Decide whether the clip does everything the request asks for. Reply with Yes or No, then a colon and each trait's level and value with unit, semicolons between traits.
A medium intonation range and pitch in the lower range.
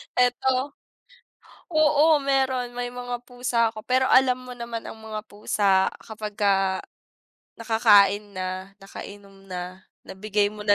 No: average, 3.8 semitones; high, 220 Hz